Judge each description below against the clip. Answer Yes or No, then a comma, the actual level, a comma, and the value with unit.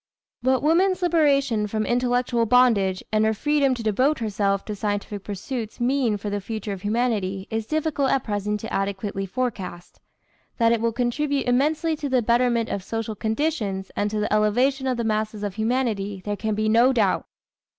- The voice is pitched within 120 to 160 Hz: No, high, 225 Hz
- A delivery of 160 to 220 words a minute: Yes, average, 180 wpm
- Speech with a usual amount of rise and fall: Yes, average, 3.7 semitones